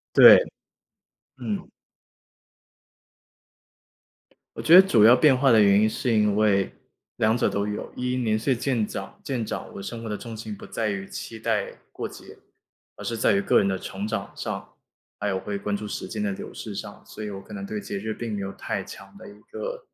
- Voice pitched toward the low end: Yes, low, 110 Hz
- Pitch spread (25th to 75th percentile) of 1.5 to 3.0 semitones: No, average, 3.7 semitones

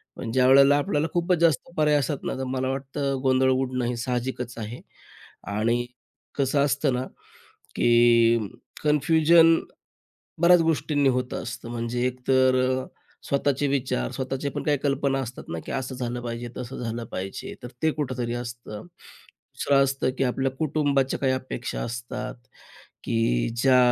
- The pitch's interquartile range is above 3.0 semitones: No, narrow, 2.5 semitones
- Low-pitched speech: Yes, low, 130 Hz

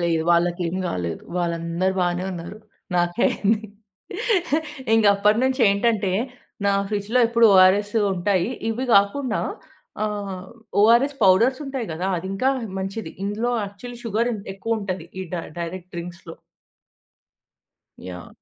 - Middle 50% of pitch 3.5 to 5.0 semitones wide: Yes, average, 4.2 semitones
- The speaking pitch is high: Yes, high, 200 Hz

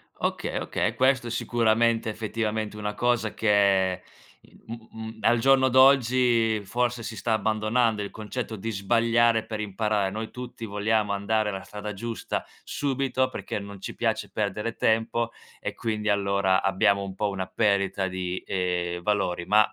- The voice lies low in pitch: Yes, low, 110 Hz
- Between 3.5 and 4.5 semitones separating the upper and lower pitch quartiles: No, narrow, 2.6 semitones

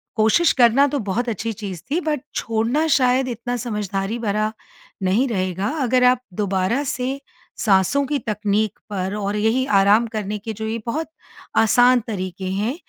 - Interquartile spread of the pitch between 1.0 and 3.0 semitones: No, average, 3.8 semitones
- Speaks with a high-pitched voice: Yes, high, 220 Hz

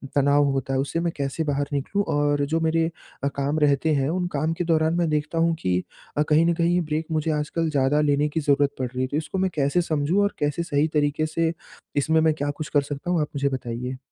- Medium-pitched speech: Yes, medium, 150 Hz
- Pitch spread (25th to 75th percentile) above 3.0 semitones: No, narrow, 2.4 semitones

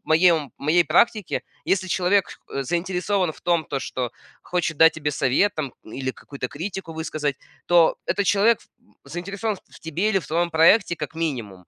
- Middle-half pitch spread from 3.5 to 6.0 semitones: Yes, average, 4.0 semitones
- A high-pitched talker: No, medium, 165 Hz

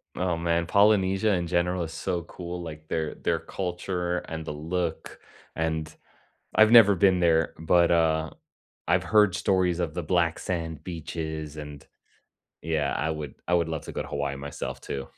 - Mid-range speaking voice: No, very low, 85 Hz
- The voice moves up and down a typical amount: No, narrow, 2.2 semitones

